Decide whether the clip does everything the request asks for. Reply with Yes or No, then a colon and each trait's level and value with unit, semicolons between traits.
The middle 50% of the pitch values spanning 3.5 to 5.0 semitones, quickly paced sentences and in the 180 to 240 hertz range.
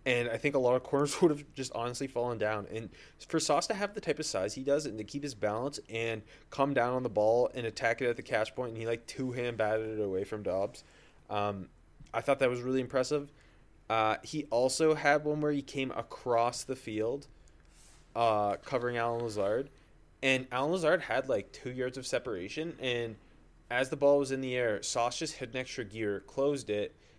No: average, 3.8 semitones; fast, 220 wpm; low, 125 Hz